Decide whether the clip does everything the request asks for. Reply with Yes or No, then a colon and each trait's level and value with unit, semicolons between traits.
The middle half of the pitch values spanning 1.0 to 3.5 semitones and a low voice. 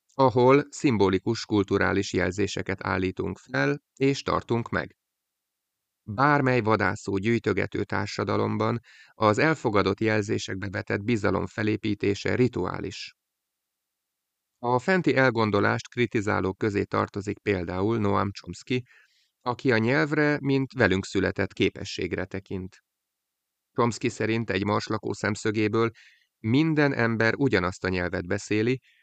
No: average, 3.9 semitones; low, 110 Hz